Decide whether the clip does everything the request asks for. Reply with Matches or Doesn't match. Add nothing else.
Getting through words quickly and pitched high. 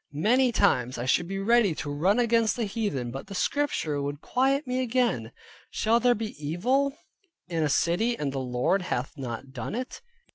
Doesn't match